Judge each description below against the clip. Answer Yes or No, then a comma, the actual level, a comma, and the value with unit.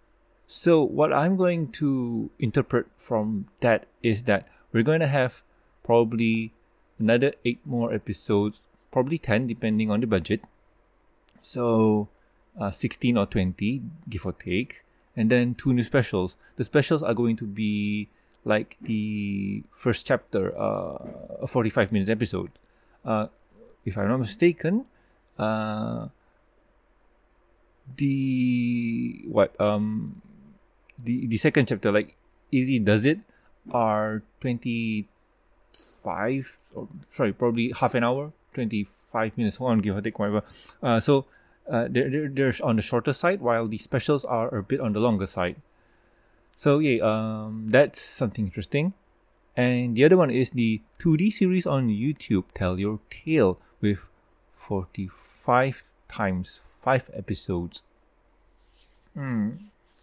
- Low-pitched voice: Yes, low, 115 Hz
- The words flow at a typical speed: No, slow, 130 wpm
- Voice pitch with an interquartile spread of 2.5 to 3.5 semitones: No, average, 3.9 semitones